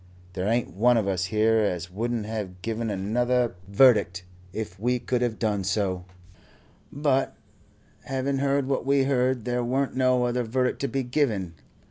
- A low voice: Yes, low, 120 Hz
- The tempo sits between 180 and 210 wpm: No, average, 160 wpm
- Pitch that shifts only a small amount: No, average, 3.9 semitones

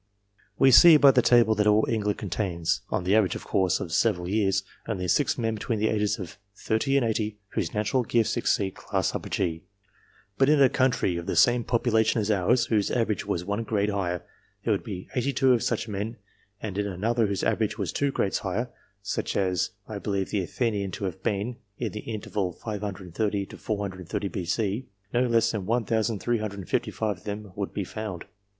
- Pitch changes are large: No, average, 2.9 semitones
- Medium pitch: No, low, 105 Hz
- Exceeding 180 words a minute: Yes, average, 190 wpm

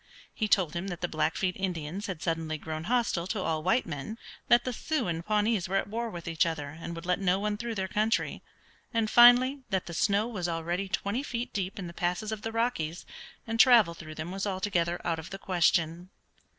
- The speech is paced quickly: Yes, fast, 215 wpm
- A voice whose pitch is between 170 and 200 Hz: Yes, medium, 185 Hz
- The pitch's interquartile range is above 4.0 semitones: Yes, average, 4.5 semitones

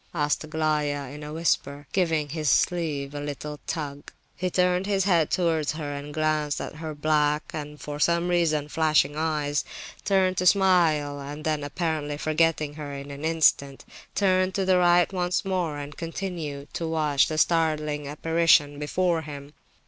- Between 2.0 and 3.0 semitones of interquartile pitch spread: Yes, narrow, 2.5 semitones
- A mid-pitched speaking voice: Yes, medium, 155 Hz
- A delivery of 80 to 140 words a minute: No, average, 165 wpm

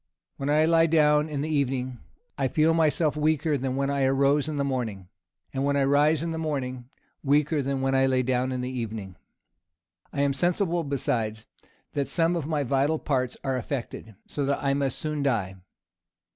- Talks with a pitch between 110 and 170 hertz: Yes, medium, 140 Hz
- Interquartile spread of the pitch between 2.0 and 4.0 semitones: Yes, average, 2.8 semitones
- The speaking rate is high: No, average, 190 wpm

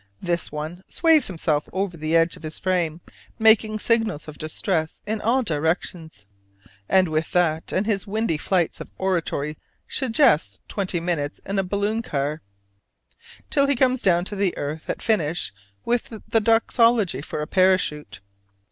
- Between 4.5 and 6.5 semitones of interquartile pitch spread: Yes, wide, 5.5 semitones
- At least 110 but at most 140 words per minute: No, average, 155 wpm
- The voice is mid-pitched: Yes, medium, 180 Hz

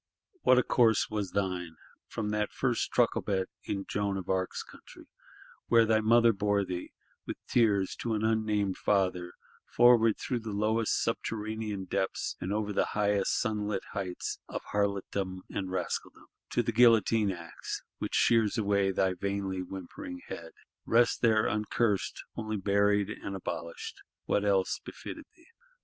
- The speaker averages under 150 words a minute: Yes, average, 140 wpm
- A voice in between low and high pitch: No, low, 105 Hz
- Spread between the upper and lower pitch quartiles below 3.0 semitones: Yes, narrow, 2.4 semitones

